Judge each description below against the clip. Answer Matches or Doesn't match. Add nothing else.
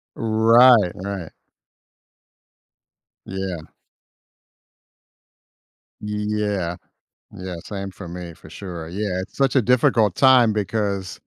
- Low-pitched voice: Matches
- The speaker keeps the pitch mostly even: Doesn't match